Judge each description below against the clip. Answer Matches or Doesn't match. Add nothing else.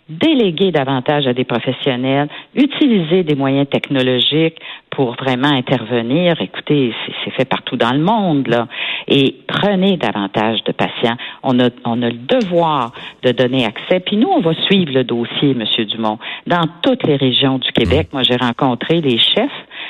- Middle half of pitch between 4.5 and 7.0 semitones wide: Matches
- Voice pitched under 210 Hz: Matches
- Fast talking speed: Doesn't match